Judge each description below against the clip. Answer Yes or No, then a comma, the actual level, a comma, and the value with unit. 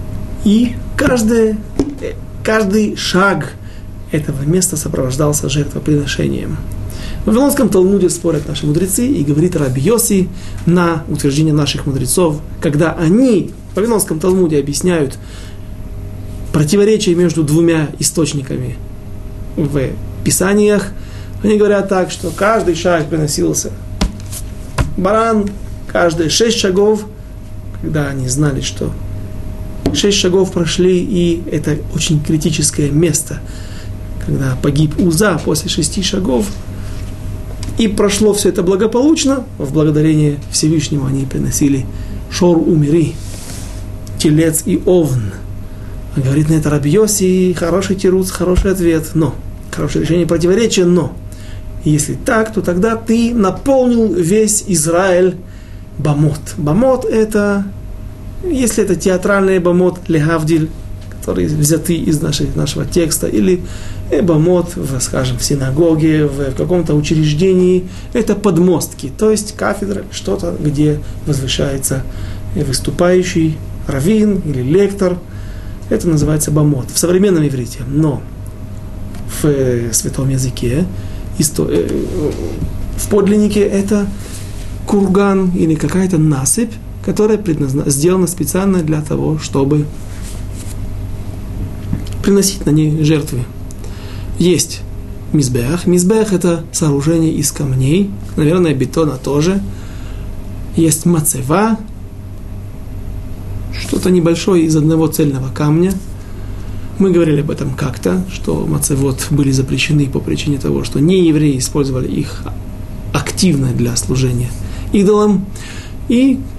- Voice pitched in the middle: Yes, medium, 150 Hz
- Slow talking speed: Yes, slow, 105 wpm